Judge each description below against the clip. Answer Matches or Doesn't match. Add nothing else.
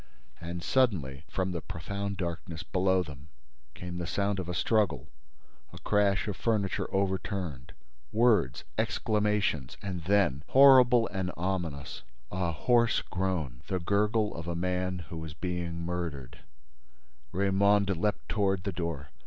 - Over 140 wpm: Doesn't match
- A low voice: Matches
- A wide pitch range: Doesn't match